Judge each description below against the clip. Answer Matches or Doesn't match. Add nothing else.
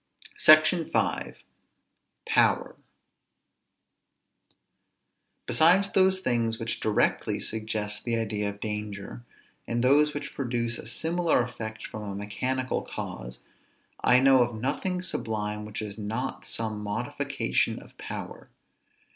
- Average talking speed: Doesn't match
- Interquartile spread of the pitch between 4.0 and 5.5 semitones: Matches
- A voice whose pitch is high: Doesn't match